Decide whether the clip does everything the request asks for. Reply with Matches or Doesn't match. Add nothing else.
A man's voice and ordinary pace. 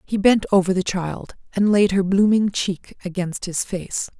Doesn't match